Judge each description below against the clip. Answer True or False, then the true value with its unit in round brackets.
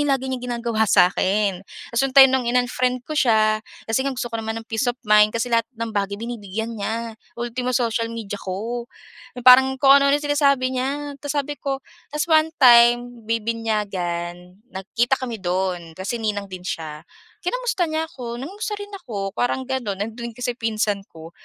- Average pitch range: True (3.6 semitones)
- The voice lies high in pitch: True (235 Hz)